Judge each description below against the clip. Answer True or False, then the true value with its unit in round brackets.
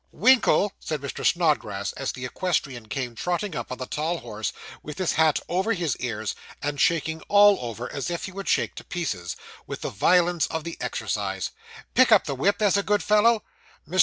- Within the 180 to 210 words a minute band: True (195 wpm)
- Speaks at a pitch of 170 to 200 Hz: False (160 Hz)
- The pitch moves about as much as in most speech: False (7.0 semitones)